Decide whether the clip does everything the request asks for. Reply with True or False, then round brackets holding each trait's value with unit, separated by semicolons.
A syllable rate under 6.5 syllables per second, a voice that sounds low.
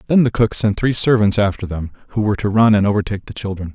False (6.9 syllables/s; 105 Hz)